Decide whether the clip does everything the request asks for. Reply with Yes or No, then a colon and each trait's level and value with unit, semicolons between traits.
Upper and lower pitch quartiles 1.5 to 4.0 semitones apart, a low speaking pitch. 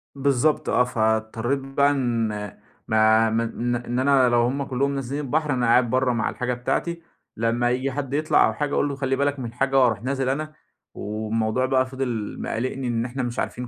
Yes: average, 2.7 semitones; low, 125 Hz